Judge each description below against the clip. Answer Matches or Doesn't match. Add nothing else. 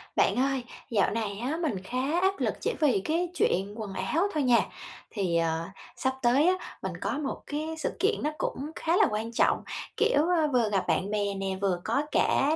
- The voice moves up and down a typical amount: Doesn't match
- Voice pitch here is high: Matches